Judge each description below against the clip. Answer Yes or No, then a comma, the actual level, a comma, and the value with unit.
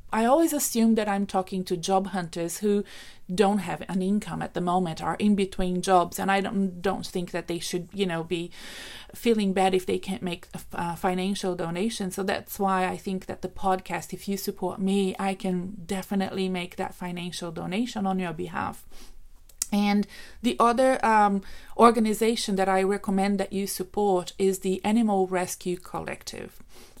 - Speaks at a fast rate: No, average, 175 wpm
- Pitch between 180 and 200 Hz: Yes, high, 190 Hz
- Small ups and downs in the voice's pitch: Yes, narrow, 1.9 semitones